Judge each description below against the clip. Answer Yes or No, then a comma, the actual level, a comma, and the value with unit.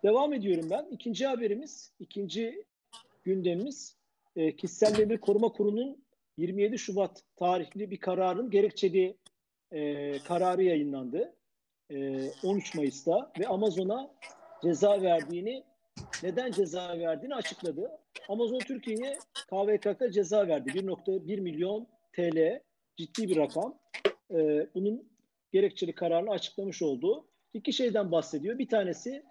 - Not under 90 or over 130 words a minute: Yes, average, 110 wpm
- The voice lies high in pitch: Yes, high, 200 Hz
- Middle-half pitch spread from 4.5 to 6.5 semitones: Yes, average, 5.3 semitones